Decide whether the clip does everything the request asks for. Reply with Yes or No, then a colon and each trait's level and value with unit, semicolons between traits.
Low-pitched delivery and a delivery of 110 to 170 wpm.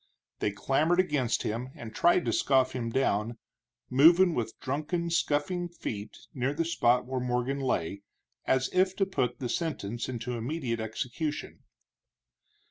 Yes: low, 130 Hz; average, 140 wpm